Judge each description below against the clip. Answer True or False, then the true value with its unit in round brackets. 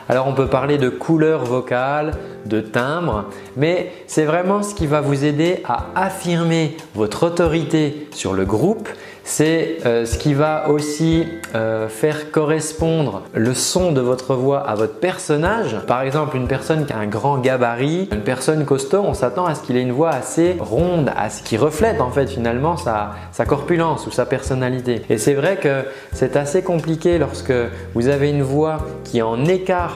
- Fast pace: False (180 wpm)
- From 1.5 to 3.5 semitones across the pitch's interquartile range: False (4.7 semitones)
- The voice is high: False (150 Hz)